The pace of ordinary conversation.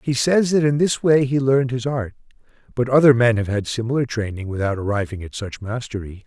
No: fast, 210 wpm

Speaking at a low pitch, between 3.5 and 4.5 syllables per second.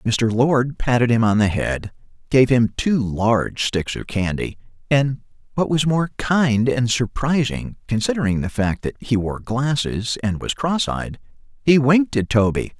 Yes: low, 120 Hz; 4.3 syllables/s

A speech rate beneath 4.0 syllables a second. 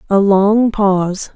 Yes: 3.5 syllables/s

